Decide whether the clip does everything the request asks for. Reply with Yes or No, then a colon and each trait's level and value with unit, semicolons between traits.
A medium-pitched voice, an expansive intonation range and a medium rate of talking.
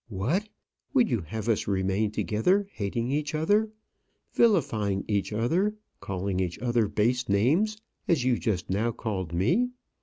No: low, 115 Hz; wide, 8.0 semitones; average, 145 wpm